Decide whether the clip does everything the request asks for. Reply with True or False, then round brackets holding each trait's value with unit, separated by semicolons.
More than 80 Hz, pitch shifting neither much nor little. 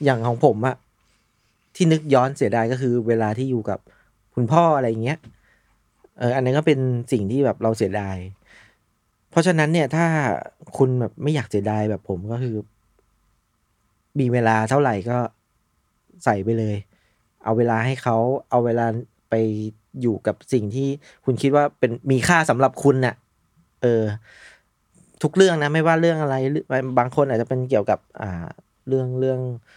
True (120 Hz; 3.5 semitones)